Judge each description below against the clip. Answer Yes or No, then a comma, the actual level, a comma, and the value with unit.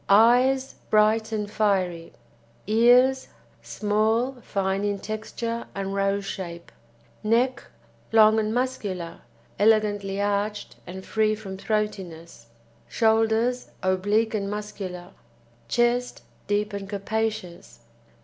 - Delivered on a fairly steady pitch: Yes, narrow, 2.2 semitones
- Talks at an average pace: No, slow, 100 wpm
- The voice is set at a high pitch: Yes, high, 210 Hz